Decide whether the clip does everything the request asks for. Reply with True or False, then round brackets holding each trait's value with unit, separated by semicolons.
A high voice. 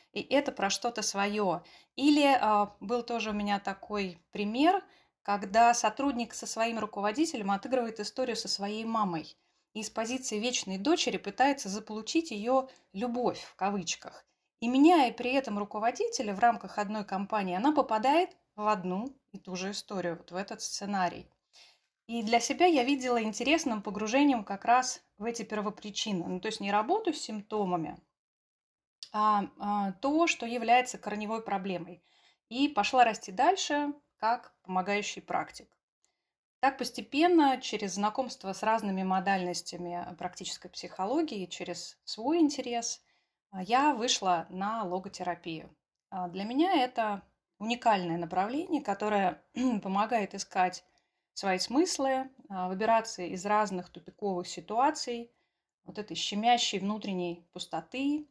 True (215 Hz)